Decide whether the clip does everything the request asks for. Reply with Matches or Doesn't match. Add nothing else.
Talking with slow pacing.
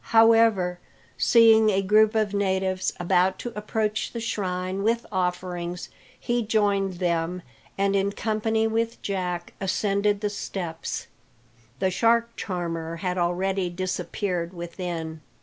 Matches